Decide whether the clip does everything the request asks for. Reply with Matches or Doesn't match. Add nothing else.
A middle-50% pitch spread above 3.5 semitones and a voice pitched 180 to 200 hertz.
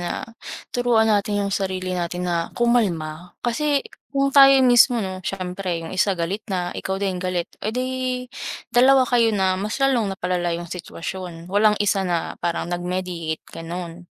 Matches